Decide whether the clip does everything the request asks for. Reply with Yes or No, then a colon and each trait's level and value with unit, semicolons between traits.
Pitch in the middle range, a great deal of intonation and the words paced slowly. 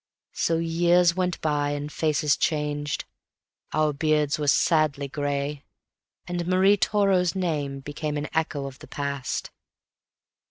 No: medium, 150 Hz; average, 2.9 semitones; slow, 125 wpm